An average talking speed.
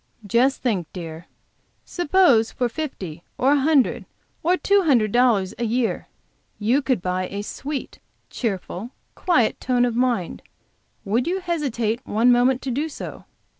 Yes: average, 145 wpm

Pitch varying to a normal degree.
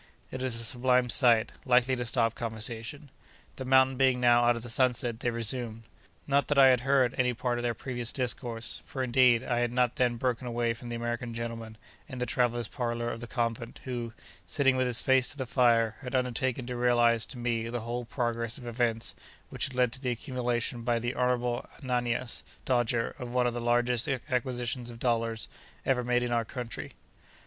No: narrow, 1.3 semitones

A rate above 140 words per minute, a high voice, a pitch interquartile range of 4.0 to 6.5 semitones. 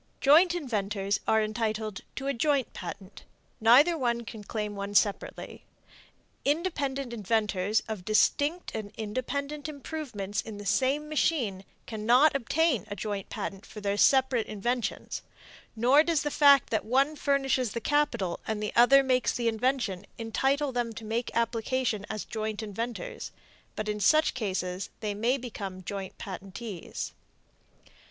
No: slow, 135 wpm; high, 230 Hz; average, 4.8 semitones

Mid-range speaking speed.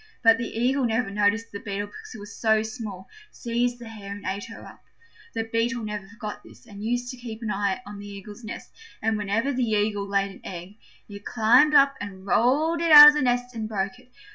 No: fast, 225 wpm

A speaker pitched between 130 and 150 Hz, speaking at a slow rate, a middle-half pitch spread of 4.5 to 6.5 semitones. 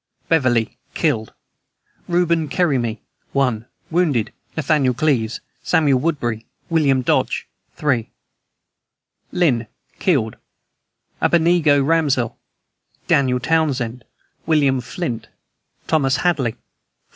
Yes: medium, 140 Hz; slow, 85 wpm; average, 5.0 semitones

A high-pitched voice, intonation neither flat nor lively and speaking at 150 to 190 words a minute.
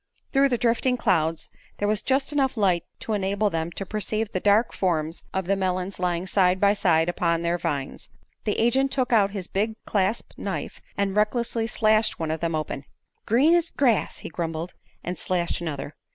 Yes: high, 195 Hz; average, 4.6 semitones; average, 180 wpm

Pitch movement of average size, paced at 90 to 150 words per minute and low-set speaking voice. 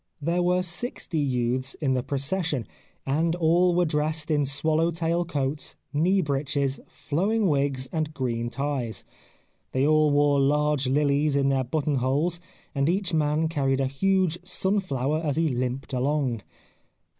No: average, 3.4 semitones; average, 145 wpm; medium, 150 Hz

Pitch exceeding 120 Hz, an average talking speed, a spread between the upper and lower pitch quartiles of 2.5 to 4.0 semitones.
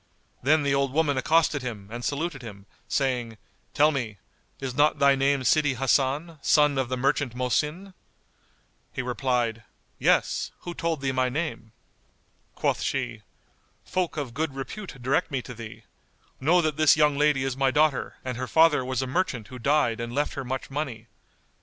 Yes: low, 135 Hz; average, 170 wpm; average, 3.0 semitones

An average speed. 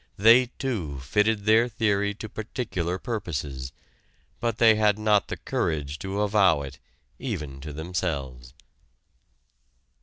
No: slow, 120 wpm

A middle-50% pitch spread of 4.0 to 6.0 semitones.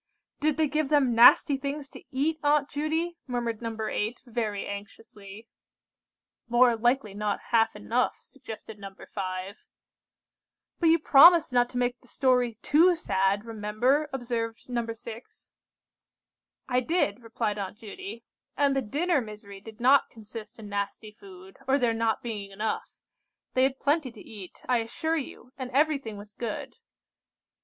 Yes: average, 4.6 semitones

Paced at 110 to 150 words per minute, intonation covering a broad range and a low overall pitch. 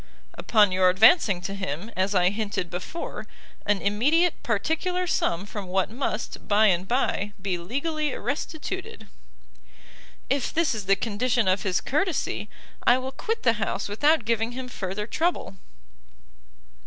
No: average, 140 wpm; wide, 6.5 semitones; high, 215 Hz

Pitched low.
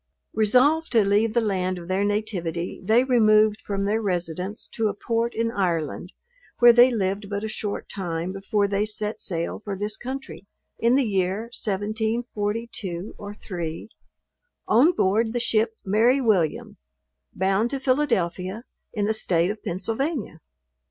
No: high, 210 Hz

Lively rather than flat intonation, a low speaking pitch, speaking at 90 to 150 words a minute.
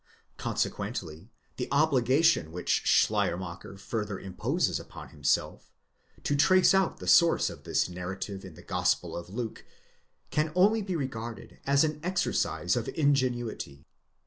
Yes: wide, 8.6 semitones; low, 120 Hz; slow, 135 wpm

